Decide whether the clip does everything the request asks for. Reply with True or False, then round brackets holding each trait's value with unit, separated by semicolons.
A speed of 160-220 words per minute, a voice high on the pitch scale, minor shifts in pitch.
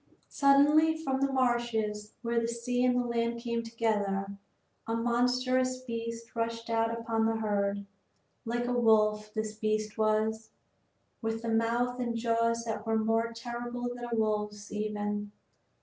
False (145 wpm; 230 Hz; 1.9 semitones)